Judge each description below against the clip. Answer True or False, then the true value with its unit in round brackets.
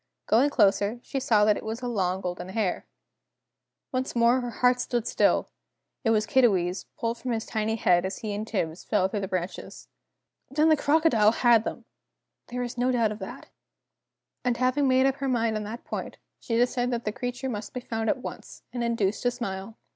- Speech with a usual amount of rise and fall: True (3.1 semitones)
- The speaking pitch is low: False (230 Hz)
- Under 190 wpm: False (200 wpm)